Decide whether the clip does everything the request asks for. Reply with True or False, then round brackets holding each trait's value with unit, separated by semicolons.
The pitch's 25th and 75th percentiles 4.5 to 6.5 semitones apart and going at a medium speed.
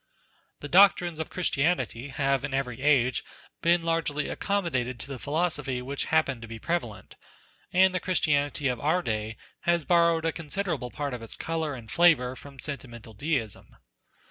True (4.8 semitones; 160 wpm)